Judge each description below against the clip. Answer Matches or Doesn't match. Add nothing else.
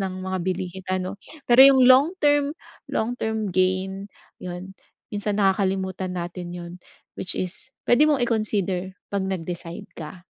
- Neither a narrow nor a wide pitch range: Matches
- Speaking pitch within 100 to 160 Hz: Doesn't match